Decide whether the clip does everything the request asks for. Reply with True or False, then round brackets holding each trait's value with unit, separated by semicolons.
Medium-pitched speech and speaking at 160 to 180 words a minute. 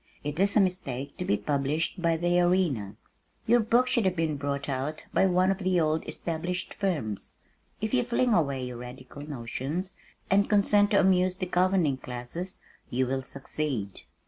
True (165 Hz; 175 wpm)